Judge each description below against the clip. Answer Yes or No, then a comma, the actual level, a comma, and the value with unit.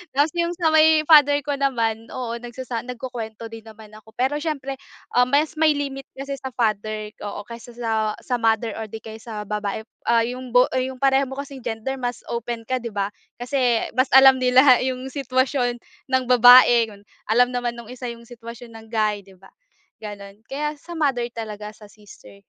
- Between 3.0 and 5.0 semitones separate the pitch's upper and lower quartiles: Yes, average, 3.3 semitones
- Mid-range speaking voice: No, high, 245 Hz